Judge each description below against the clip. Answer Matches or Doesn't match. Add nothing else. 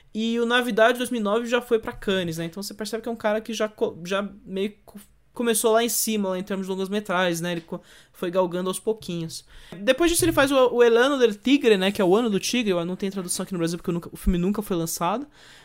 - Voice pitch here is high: Matches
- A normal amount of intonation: Matches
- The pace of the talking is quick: Matches